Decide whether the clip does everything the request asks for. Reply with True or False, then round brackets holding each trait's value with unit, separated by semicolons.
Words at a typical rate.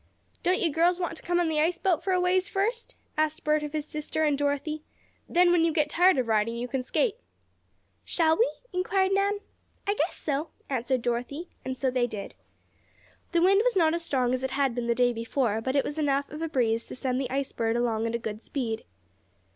False (225 wpm)